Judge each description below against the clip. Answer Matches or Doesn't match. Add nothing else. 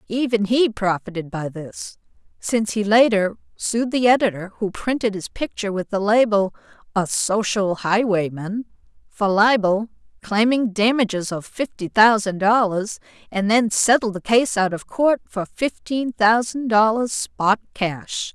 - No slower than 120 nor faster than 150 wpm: Matches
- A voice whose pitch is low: Doesn't match